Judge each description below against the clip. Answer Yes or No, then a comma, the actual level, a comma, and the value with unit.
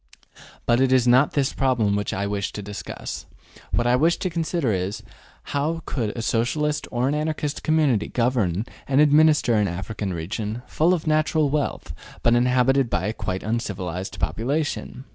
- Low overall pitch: Yes, low, 125 Hz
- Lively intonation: Yes, wide, 6.3 semitones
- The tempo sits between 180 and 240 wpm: No, average, 165 wpm